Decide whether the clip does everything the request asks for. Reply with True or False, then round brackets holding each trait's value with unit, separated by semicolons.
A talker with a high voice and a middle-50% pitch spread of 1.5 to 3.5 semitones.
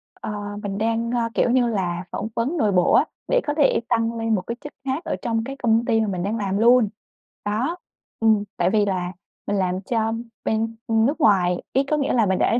True (225 Hz; 3.1 semitones)